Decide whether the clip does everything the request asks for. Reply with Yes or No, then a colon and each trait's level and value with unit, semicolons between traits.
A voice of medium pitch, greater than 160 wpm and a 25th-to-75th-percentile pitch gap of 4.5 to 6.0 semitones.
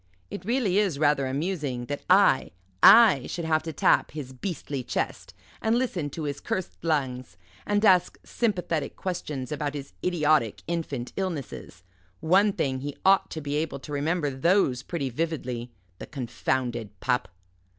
No: medium, 150 Hz; average, 150 wpm; average, 5.3 semitones